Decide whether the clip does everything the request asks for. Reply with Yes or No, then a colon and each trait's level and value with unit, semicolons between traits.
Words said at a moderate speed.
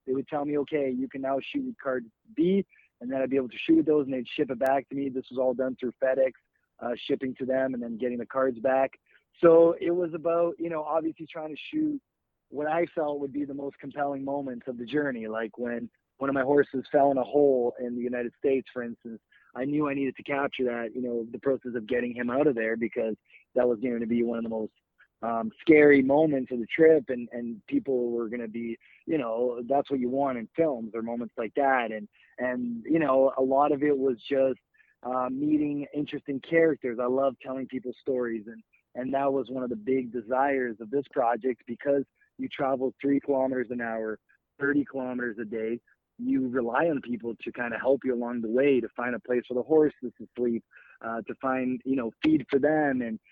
No: fast, 230 wpm